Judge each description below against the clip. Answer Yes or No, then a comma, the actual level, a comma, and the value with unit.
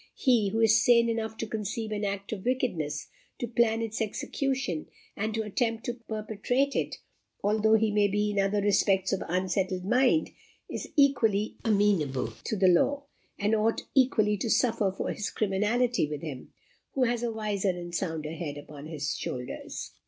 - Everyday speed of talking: Yes, average, 170 wpm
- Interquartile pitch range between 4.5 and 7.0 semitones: No, average, 3.2 semitones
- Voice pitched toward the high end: Yes, high, 210 Hz